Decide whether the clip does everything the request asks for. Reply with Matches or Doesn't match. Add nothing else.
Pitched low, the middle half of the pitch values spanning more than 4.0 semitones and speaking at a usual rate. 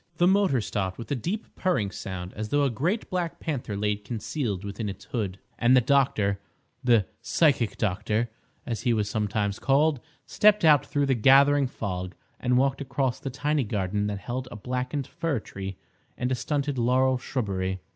Matches